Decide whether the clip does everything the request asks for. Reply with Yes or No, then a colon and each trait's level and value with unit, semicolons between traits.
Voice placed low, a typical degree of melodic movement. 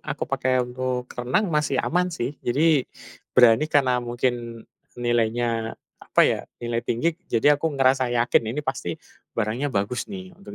Yes: low, 125 Hz; average, 3.7 semitones